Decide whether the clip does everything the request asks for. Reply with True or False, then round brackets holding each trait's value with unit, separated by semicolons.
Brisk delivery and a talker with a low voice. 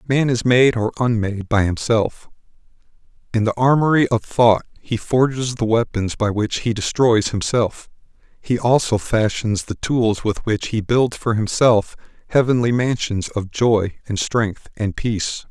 False (155 wpm; 115 Hz)